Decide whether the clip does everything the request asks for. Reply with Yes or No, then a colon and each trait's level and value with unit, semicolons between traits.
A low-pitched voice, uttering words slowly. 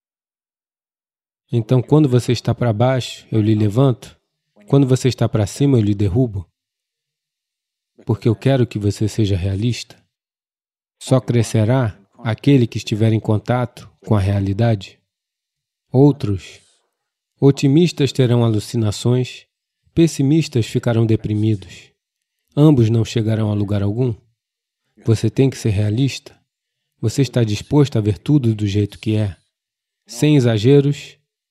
Yes: low, 115 Hz; slow, 120 wpm